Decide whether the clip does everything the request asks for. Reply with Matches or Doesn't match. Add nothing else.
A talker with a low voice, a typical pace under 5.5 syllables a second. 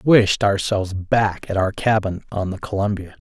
Matches